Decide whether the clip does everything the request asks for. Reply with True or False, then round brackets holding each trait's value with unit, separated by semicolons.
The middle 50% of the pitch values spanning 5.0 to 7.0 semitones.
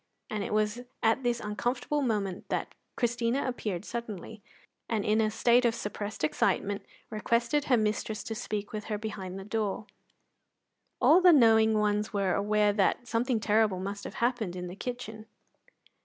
False (2.4 semitones)